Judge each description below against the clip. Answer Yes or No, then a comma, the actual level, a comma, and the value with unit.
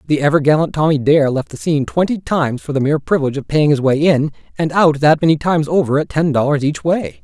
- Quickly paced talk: Yes, fast, 250 wpm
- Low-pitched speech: No, medium, 145 Hz